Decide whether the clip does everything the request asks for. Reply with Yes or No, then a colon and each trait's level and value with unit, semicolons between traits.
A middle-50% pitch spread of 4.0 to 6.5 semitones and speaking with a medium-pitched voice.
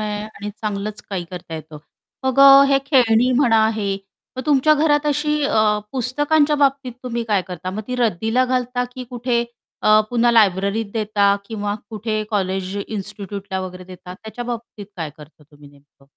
No: average, 4.5 semitones; high, 220 Hz